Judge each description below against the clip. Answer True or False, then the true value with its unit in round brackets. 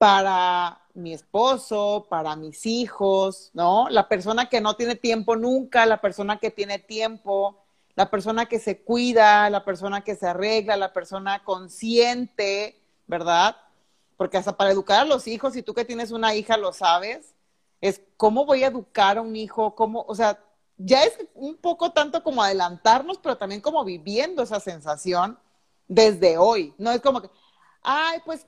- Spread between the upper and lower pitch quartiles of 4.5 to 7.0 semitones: False (3.3 semitones)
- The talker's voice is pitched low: False (215 Hz)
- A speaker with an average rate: True (170 wpm)